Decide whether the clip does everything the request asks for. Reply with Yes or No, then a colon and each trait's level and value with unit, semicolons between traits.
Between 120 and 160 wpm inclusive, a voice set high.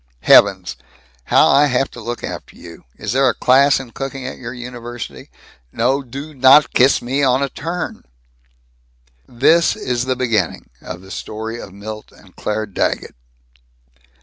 No: average, 155 wpm; low, 125 Hz